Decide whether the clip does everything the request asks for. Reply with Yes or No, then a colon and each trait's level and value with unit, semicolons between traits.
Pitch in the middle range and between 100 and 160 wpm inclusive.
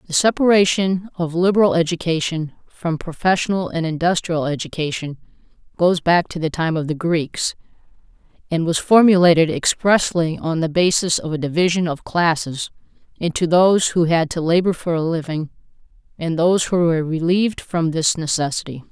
Yes: medium, 170 Hz; average, 150 wpm